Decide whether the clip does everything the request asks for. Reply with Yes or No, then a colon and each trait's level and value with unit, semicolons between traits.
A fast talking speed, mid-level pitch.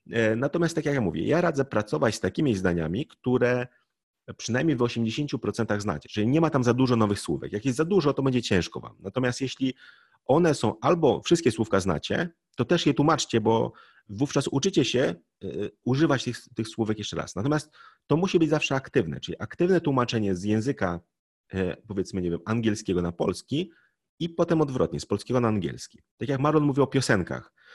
No: fast, 180 wpm; low, 125 Hz